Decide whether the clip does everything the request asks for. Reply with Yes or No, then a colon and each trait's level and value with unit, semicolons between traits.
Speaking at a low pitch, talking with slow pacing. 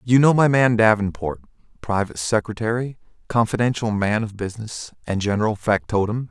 Yes: low, 110 Hz; slow, 125 wpm